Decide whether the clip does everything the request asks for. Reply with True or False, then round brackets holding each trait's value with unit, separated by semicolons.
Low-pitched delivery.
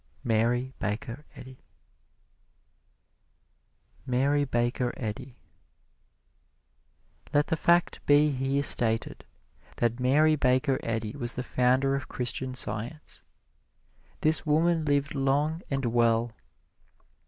True (130 Hz)